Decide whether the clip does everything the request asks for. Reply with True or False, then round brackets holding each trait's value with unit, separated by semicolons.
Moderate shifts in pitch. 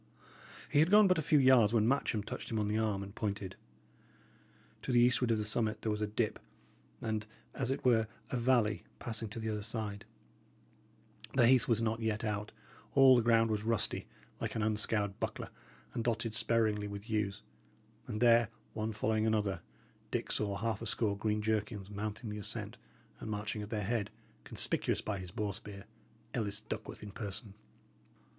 False (1.7 semitones)